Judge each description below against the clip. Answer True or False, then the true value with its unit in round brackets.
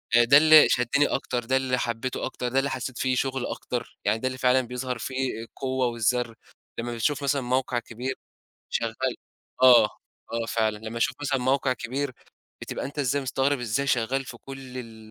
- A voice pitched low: True (125 Hz)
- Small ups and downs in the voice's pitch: True (2.1 semitones)